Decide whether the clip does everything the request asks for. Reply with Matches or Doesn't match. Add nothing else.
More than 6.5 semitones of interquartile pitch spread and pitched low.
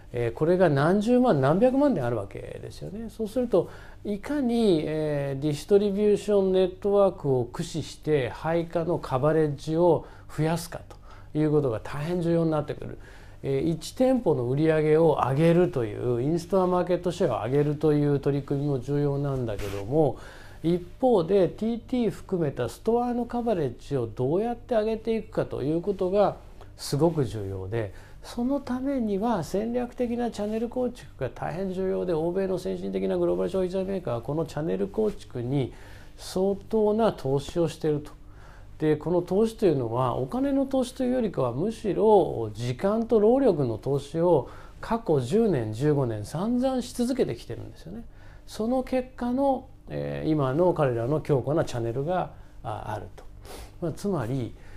Doesn't match